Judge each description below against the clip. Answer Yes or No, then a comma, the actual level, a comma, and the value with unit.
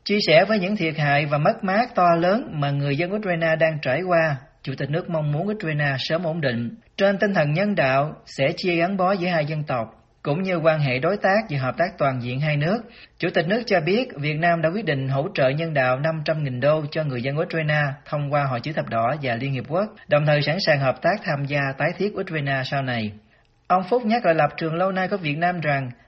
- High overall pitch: No, medium, 155 Hz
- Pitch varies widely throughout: No, average, 4.3 semitones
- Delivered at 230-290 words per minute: Yes, fast, 250 wpm